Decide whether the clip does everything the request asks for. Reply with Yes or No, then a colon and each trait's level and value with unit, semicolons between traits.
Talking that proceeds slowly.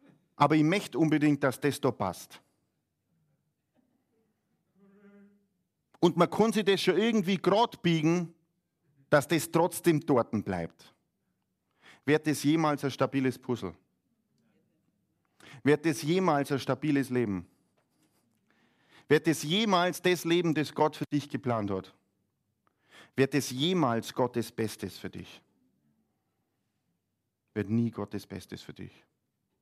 Yes: slow, 120 wpm